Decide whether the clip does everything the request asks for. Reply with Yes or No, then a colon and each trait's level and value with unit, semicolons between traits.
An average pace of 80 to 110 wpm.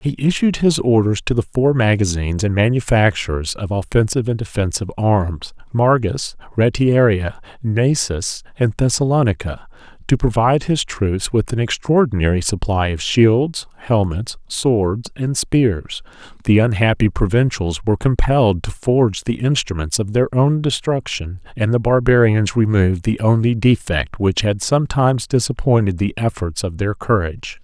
No: slow, 135 wpm